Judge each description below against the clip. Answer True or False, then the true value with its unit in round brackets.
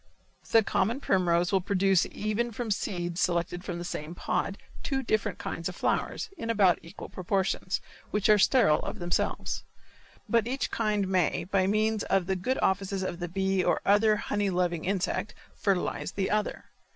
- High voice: True (195 Hz)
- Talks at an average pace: True (170 wpm)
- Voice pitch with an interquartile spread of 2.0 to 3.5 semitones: True (3.0 semitones)